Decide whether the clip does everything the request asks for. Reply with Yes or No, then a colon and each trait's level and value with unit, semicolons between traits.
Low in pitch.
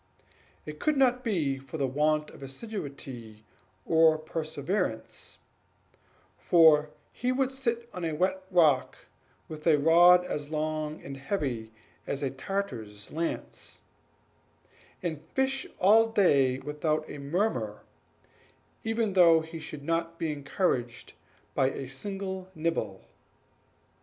No: medium, 155 Hz